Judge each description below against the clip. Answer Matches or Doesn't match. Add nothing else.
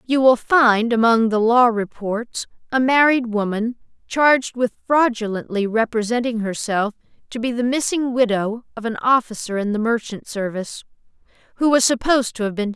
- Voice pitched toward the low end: Doesn't match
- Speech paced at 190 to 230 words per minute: Doesn't match